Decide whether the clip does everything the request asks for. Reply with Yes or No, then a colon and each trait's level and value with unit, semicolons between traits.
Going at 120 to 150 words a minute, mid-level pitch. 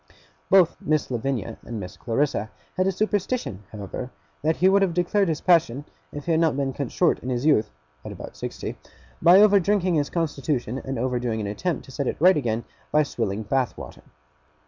No: average, 200 wpm; medium, 145 Hz